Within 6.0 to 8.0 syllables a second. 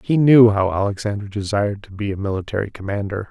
Yes: 6.3 syllables/s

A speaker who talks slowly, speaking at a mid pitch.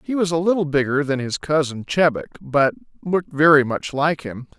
No: average, 195 wpm; medium, 150 Hz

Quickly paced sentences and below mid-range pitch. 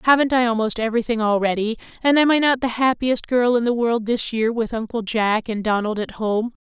No: fast, 215 wpm; high, 230 Hz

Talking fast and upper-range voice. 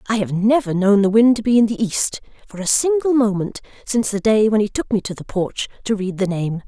Yes: fast, 260 wpm; high, 210 Hz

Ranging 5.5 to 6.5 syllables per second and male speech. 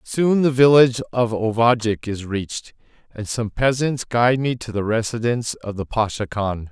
No: 4.9 syllables/s; male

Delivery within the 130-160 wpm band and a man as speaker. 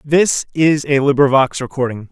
Yes: average, 140 wpm; male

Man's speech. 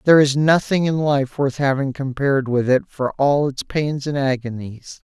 Yes: male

